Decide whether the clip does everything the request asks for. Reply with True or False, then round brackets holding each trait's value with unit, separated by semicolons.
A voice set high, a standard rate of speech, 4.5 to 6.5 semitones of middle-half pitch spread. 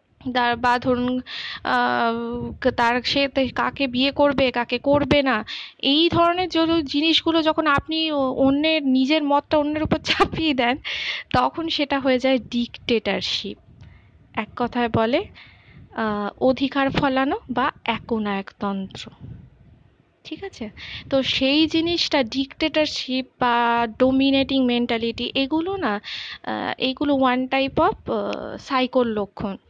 False (265 Hz; 105 wpm; 3.4 semitones)